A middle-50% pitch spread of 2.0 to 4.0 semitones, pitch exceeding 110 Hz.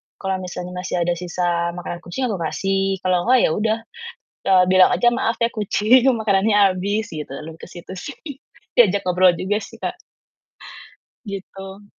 Yes: average, 2.9 semitones; high, 190 Hz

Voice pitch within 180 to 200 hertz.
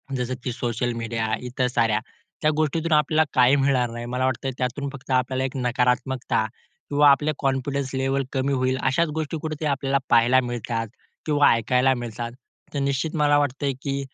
No: low, 130 Hz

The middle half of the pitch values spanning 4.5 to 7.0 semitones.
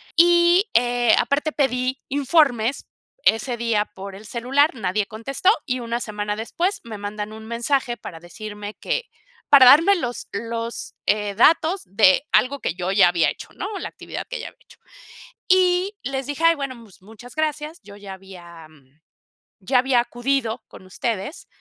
Yes: wide, 5.4 semitones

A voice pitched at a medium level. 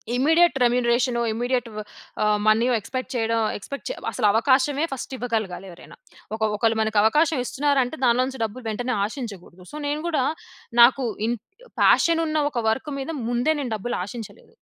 No: high, 245 Hz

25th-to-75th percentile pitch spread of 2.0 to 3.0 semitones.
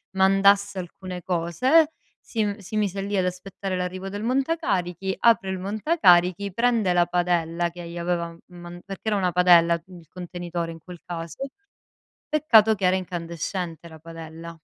Yes: average, 2.7 semitones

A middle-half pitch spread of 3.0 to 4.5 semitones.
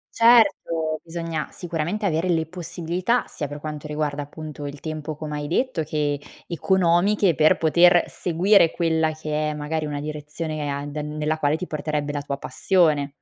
No: narrow, 2.4 semitones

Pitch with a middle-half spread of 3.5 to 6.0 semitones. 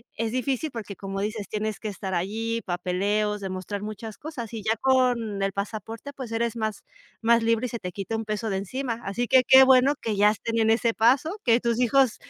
No: average, 2.8 semitones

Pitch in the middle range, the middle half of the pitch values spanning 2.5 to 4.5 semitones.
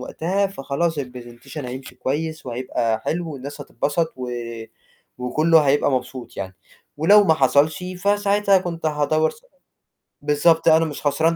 Yes: medium, 150 Hz; average, 4.1 semitones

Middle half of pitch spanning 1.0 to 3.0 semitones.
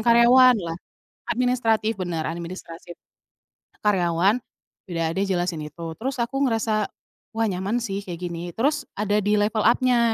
No: average, 5.1 semitones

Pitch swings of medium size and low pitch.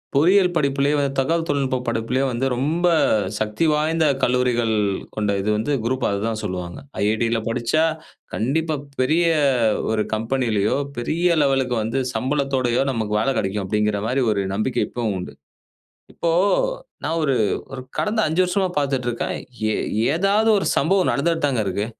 No: wide, 5.8 semitones; low, 130 Hz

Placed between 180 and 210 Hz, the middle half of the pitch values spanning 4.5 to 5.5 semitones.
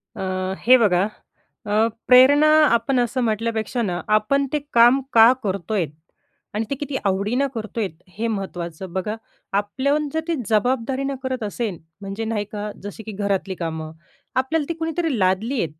No: high, 220 Hz; average, 4.8 semitones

